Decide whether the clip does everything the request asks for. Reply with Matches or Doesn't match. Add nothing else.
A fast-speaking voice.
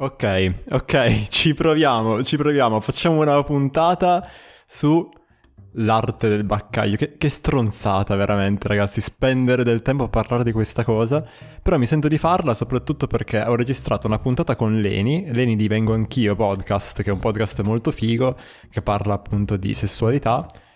Doesn't match